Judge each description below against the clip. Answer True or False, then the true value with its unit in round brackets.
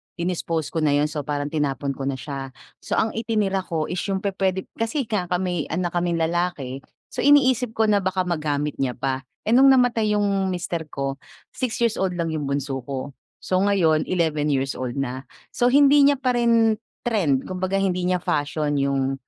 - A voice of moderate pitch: True (175 Hz)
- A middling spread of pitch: False (6.4 semitones)